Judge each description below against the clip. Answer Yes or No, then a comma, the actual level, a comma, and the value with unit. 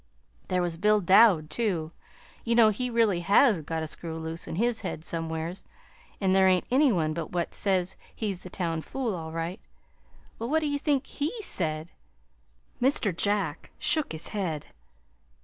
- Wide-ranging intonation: Yes, wide, 5.9 semitones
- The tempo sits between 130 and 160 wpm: No, average, 170 wpm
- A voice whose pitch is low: No, medium, 185 Hz